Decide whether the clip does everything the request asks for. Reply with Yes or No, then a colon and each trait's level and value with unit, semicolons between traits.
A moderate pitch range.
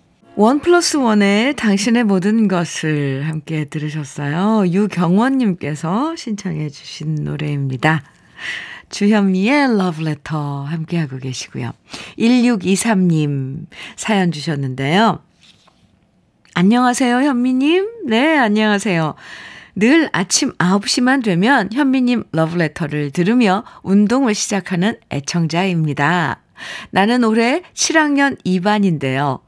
No: wide, 7.1 semitones